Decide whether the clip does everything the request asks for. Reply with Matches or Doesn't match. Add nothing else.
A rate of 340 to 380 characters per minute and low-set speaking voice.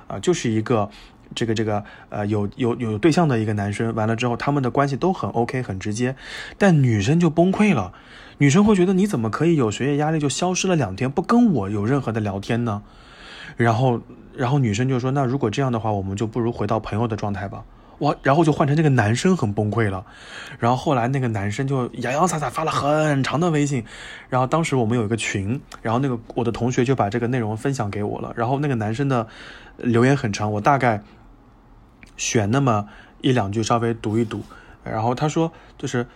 Doesn't match